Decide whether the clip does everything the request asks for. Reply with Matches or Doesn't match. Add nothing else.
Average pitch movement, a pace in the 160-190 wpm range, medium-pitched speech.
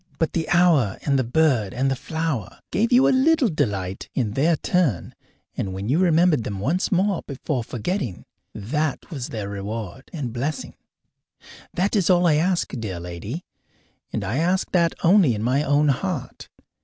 Doesn't match